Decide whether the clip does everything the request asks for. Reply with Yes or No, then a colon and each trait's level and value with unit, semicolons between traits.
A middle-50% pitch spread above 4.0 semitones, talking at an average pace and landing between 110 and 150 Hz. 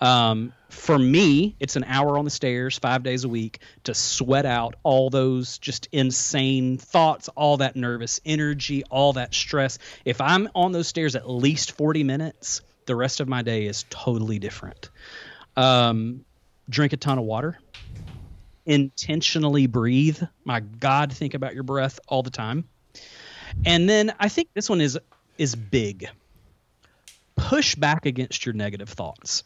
No: average, 3.4 semitones; average, 155 wpm; low, 135 Hz